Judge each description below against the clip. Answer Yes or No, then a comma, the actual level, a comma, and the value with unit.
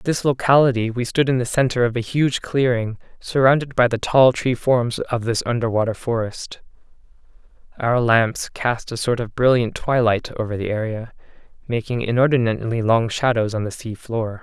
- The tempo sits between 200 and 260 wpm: No, average, 165 wpm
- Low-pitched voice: Yes, low, 120 Hz